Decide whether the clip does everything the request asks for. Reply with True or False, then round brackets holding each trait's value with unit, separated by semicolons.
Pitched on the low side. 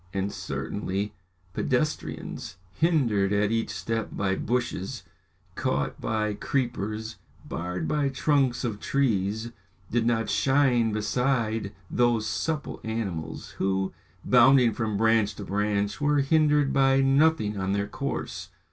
True (115 Hz)